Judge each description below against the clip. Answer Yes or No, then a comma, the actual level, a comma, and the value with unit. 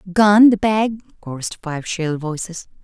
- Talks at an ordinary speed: No, slow, 125 wpm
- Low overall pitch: No, medium, 185 Hz